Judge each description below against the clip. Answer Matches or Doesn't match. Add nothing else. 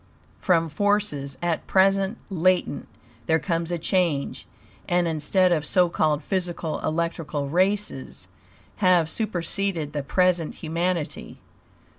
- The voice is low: Doesn't match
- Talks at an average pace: Doesn't match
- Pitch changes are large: Doesn't match